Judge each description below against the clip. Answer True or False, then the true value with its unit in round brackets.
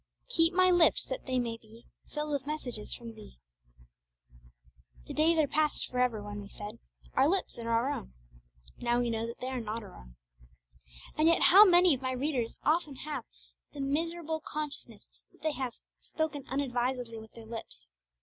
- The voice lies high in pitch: True (260 Hz)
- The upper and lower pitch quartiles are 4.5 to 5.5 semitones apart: True (5.1 semitones)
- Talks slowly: False (180 wpm)